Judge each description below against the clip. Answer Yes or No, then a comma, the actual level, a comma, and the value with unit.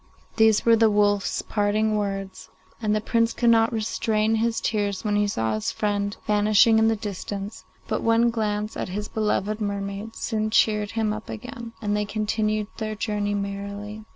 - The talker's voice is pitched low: No, high, 210 Hz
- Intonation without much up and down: Yes, narrow, 1.4 semitones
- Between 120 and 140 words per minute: No, average, 180 wpm